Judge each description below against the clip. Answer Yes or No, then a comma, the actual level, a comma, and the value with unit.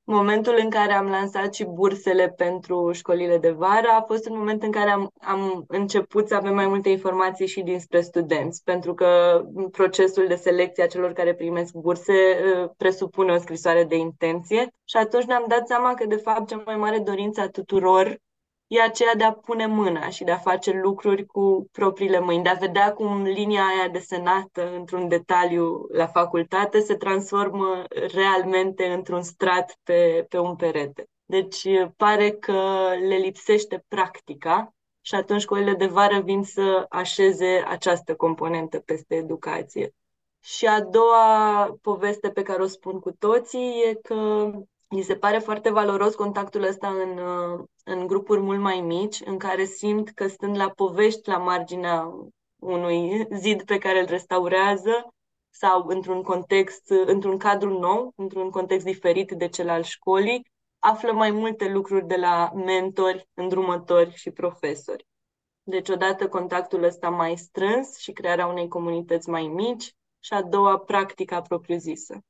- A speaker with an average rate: Yes, average, 155 wpm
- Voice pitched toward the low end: No, high, 190 Hz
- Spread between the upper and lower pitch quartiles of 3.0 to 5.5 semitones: No, narrow, 2.4 semitones